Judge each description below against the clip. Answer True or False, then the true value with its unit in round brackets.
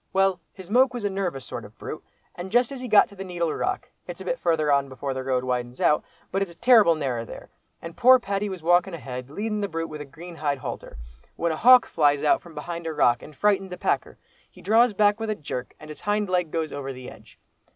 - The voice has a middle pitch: True (170 Hz)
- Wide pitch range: True (5.9 semitones)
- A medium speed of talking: False (250 wpm)